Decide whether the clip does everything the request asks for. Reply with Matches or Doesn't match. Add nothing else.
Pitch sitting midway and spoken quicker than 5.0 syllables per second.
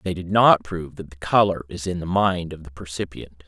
Doesn't match